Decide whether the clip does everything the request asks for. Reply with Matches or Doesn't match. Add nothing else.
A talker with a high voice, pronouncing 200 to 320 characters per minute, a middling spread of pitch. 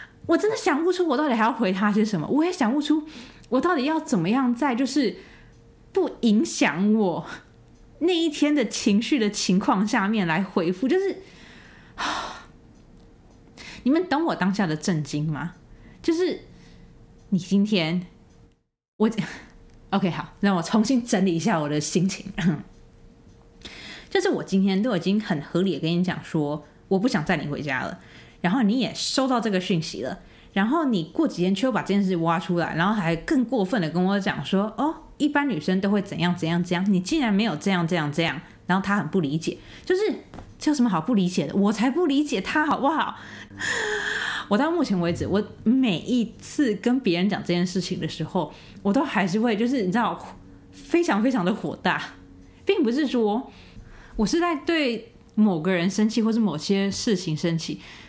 Doesn't match